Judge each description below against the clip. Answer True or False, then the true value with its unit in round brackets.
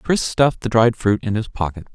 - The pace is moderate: False (245 wpm)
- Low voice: True (115 Hz)